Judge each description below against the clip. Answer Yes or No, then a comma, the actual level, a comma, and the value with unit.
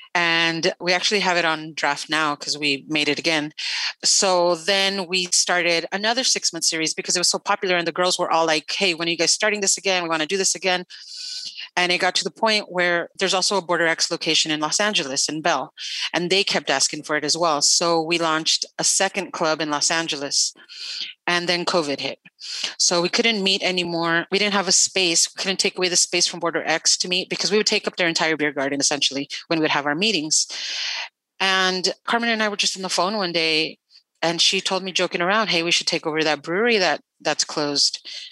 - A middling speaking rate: No, fast, 235 wpm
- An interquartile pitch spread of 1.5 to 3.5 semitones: Yes, average, 3.2 semitones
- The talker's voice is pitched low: No, medium, 175 Hz